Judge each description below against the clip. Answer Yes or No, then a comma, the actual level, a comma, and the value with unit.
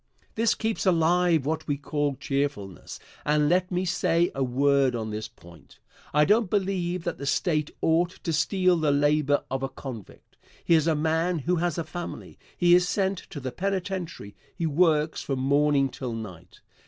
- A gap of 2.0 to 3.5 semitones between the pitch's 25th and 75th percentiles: No, average, 4.2 semitones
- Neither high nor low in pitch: Yes, medium, 155 Hz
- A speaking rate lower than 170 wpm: No, average, 180 wpm